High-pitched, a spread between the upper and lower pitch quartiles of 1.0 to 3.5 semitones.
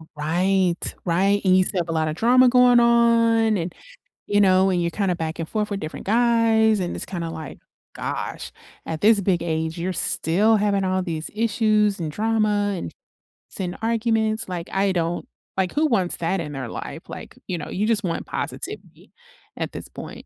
No: high, 195 Hz; average, 4.4 semitones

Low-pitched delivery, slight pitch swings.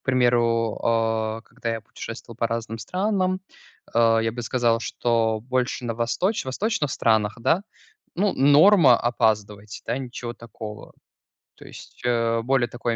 Yes: low, 115 Hz; narrow, 2.3 semitones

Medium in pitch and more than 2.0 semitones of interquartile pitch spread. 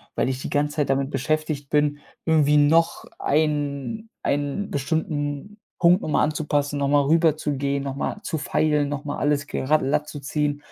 No: medium, 145 Hz; narrow, 1.5 semitones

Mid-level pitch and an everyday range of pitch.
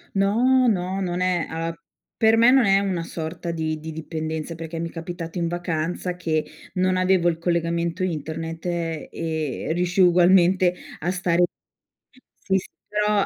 No: medium, 175 Hz; narrow, 2.2 semitones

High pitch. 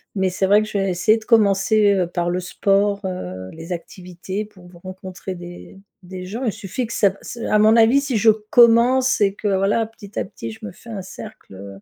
Yes: high, 195 Hz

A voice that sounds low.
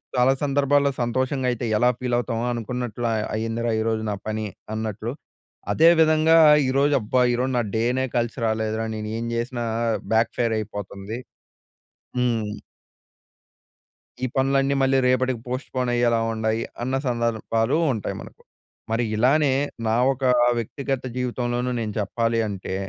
Yes: low, 120 Hz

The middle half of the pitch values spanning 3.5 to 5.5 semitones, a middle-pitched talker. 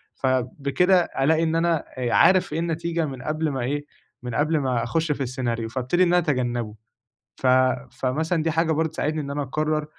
Yes: average, 4.1 semitones; medium, 150 Hz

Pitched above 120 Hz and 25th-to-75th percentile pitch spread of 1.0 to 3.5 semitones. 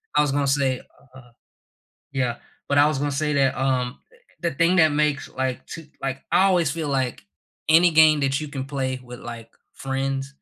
Yes: medium, 140 Hz; narrow, 2.5 semitones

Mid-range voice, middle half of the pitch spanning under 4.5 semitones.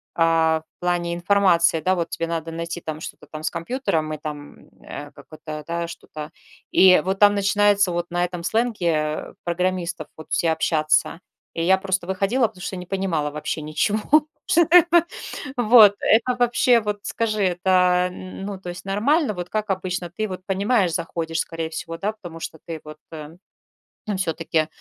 Yes: medium, 180 Hz; average, 3.7 semitones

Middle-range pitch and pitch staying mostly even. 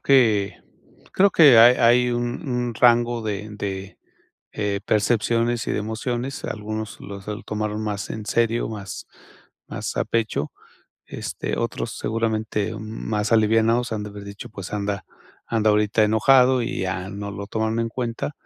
No: low, 110 Hz; narrow, 2.3 semitones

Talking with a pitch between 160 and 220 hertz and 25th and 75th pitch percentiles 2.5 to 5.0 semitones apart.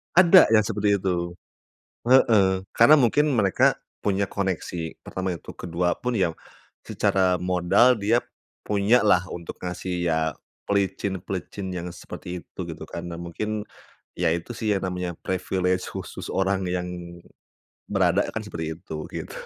No: very low, 95 Hz; average, 2.8 semitones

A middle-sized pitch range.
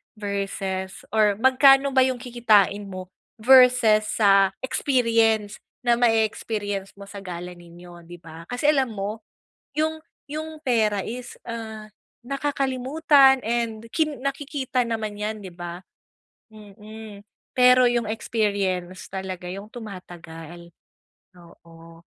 Yes: average, 4.7 semitones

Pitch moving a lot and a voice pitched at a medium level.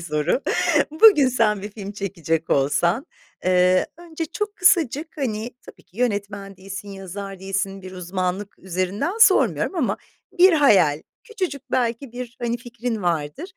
No: wide, 6.7 semitones; high, 205 Hz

